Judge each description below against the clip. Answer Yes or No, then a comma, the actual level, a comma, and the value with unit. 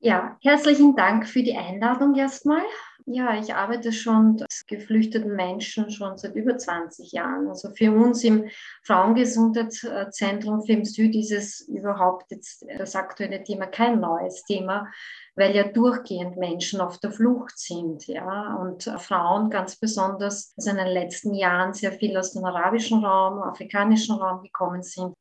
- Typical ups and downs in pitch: Yes, average, 3.4 semitones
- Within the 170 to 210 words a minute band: No, average, 150 wpm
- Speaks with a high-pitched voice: Yes, high, 205 Hz